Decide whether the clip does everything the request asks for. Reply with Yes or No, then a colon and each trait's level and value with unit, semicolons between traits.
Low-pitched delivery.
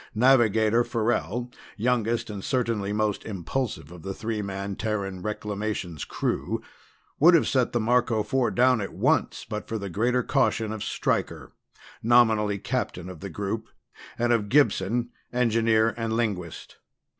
Yes: low, 110 Hz